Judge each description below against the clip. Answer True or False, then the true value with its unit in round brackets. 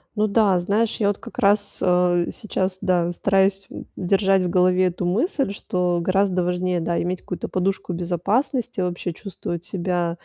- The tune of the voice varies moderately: False (2.0 semitones)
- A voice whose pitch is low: False (185 Hz)